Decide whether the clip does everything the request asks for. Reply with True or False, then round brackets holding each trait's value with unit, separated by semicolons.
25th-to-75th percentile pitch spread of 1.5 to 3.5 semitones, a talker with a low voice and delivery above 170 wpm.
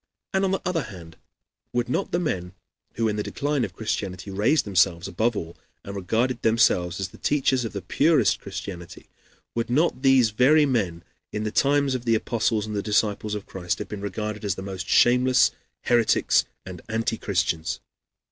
False (4.7 semitones; 110 Hz; 180 wpm)